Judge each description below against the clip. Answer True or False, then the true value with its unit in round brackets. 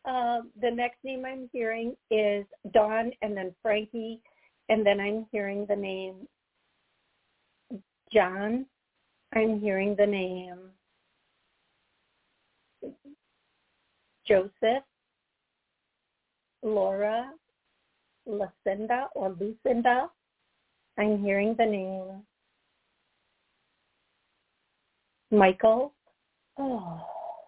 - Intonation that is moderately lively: True (3.4 semitones)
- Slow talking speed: True (70 wpm)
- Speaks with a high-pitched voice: True (220 Hz)